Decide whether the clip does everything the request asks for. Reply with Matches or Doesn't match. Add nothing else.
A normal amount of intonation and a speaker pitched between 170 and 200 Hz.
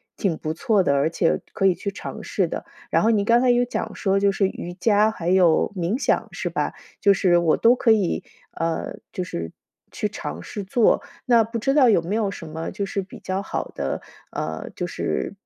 Matches